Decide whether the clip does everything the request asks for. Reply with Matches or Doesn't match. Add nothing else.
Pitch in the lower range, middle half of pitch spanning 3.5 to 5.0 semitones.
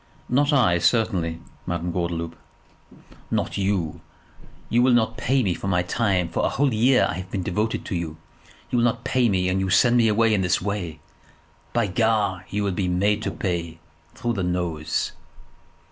Matches